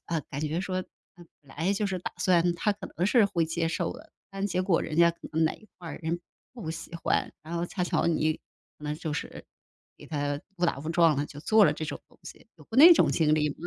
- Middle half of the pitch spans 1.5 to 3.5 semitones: Yes, average, 2.9 semitones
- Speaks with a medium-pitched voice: Yes, medium, 170 Hz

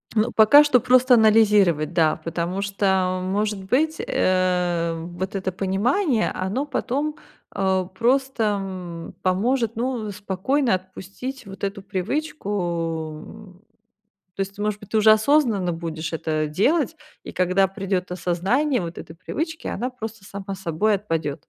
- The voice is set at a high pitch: Yes, high, 195 Hz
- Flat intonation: No, average, 4.2 semitones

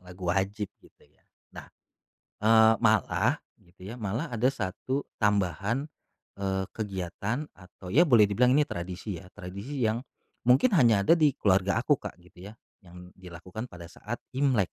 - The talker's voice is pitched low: Yes, low, 105 Hz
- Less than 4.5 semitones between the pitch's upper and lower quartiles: No, average, 4.9 semitones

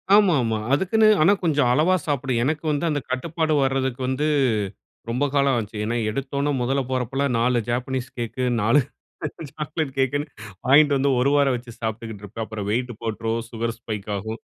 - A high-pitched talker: No, low, 130 Hz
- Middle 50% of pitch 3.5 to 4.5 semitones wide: Yes, average, 3.9 semitones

